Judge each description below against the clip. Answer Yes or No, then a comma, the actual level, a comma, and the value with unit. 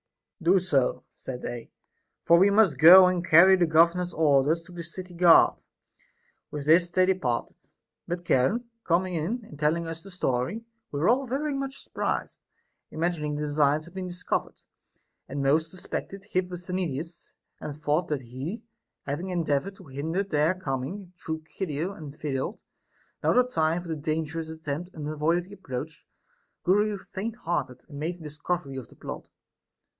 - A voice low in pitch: No, medium, 165 Hz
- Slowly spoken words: No, average, 160 wpm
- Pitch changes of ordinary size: Yes, average, 3.7 semitones